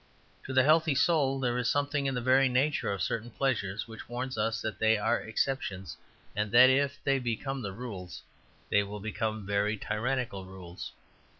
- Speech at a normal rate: Yes, average, 175 wpm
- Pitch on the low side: Yes, low, 120 Hz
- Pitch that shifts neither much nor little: Yes, average, 4.4 semitones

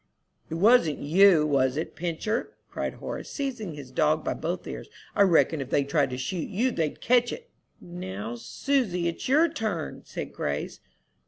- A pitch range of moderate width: No, wide, 7.2 semitones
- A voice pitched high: No, medium, 170 Hz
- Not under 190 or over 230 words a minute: No, average, 170 wpm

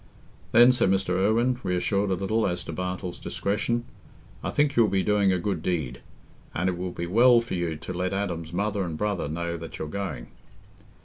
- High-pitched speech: No, very low, 95 Hz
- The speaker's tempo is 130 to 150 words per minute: No, average, 195 wpm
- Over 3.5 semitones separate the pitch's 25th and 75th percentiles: No, average, 3.2 semitones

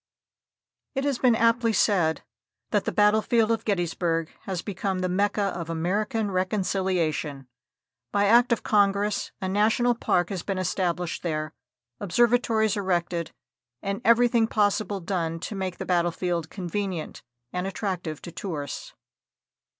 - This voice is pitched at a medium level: No, high, 195 Hz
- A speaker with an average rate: No, slow, 130 wpm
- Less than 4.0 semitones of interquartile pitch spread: Yes, average, 3.6 semitones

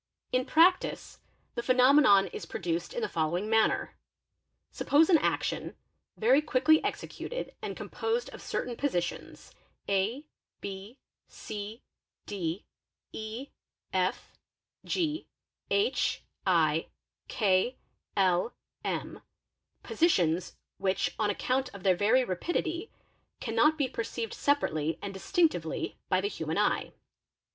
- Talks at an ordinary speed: No, slow, 115 wpm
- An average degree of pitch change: No, wide, 7.4 semitones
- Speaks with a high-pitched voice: Yes, high, 225 Hz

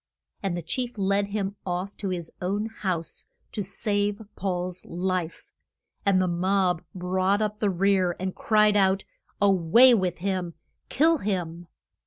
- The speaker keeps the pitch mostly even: Yes, narrow, 2.3 semitones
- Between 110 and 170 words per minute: Yes, average, 150 wpm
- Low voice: No, high, 190 Hz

